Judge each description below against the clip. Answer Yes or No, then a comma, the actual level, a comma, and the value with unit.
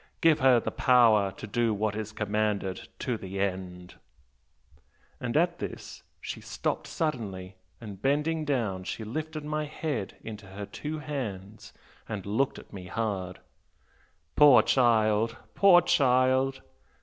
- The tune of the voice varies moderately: No, wide, 5.8 semitones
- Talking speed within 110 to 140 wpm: Yes, slow, 135 wpm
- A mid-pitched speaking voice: No, low, 115 Hz